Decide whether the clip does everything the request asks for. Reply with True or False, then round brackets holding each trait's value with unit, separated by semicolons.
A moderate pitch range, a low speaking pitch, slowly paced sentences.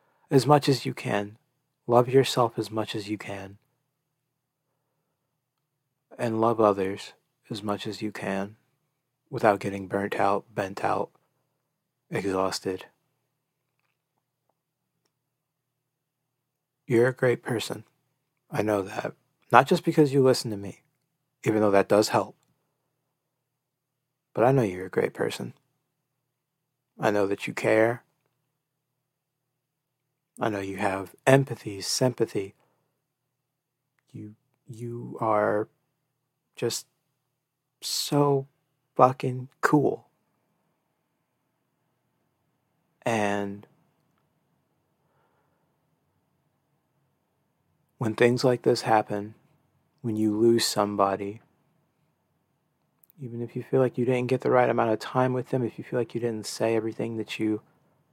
True (4.6 semitones; 130 Hz; 110 wpm)